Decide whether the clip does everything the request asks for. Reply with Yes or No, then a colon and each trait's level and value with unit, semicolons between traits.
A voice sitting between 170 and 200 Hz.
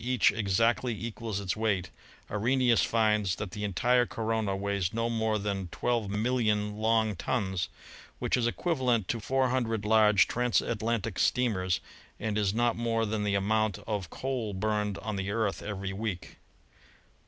No: low, 110 Hz